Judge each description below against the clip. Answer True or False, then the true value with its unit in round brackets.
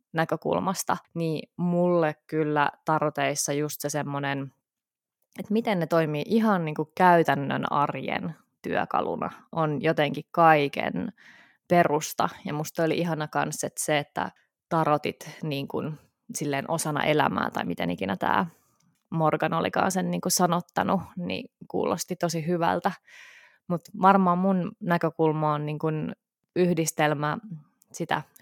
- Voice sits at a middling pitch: True (160 Hz)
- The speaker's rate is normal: True (120 wpm)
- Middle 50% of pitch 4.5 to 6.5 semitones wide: False (2.9 semitones)